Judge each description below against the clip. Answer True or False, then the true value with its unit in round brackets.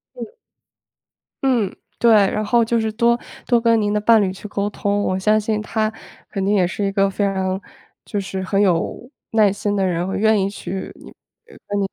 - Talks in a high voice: True (205 Hz)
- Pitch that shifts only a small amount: True (2.2 semitones)